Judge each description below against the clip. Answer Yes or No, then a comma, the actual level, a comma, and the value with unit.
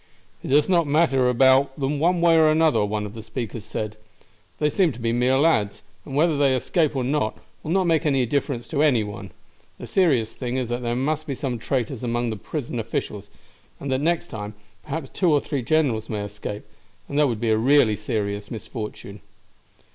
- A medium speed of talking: No, fast, 210 wpm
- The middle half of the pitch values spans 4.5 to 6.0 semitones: Yes, average, 5.2 semitones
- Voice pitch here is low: Yes, low, 130 Hz